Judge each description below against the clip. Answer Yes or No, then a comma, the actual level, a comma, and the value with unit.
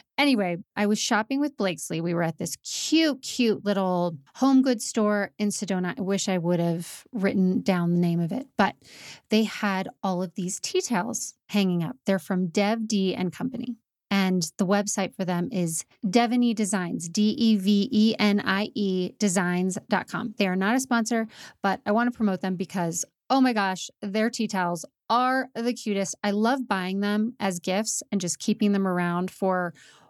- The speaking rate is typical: Yes, average, 175 wpm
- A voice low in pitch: No, high, 200 Hz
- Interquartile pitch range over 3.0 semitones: Yes, average, 3.4 semitones